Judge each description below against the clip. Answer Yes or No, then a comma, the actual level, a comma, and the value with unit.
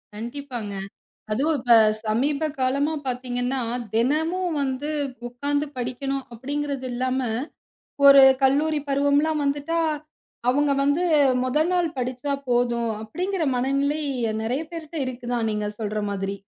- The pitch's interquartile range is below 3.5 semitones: Yes, average, 3.1 semitones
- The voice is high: Yes, very high, 275 Hz